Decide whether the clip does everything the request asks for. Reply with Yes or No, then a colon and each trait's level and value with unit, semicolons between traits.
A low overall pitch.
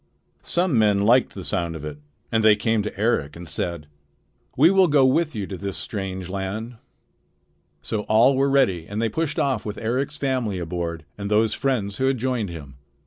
Yes: low, 110 Hz